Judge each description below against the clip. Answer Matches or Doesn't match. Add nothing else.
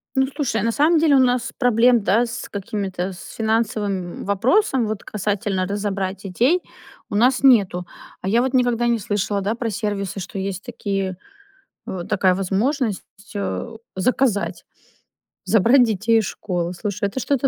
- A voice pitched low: Doesn't match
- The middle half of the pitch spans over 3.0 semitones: Matches